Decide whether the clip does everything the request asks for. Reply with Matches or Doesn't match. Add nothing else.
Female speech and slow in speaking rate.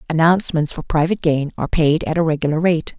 Doesn't match